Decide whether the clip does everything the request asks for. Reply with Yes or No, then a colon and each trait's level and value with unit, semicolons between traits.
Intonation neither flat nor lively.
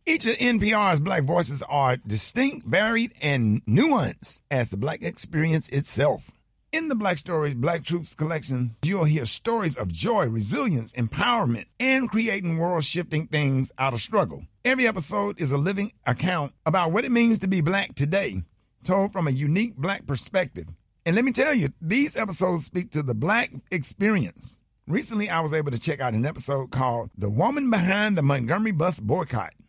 No: wide, 7.6 semitones